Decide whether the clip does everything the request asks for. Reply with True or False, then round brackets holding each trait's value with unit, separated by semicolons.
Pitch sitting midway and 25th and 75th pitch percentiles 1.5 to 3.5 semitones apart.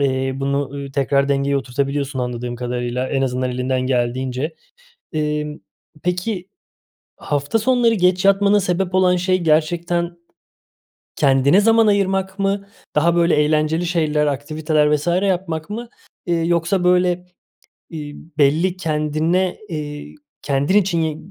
False (155 Hz; 4.6 semitones)